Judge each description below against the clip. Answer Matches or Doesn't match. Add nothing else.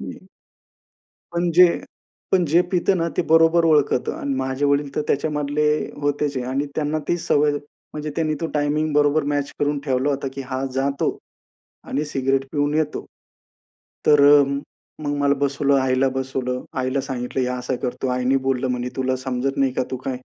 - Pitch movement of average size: Doesn't match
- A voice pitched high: Doesn't match